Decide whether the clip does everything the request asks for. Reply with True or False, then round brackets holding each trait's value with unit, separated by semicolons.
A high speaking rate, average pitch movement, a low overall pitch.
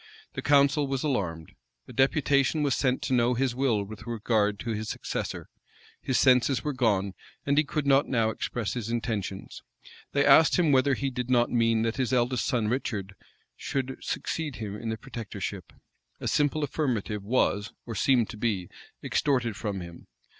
False (175 wpm; 3.9 semitones; 120 Hz)